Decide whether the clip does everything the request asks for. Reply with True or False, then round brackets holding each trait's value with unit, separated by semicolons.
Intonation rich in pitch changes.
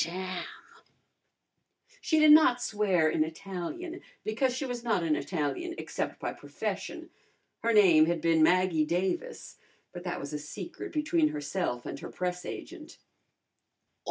True (7.0 semitones)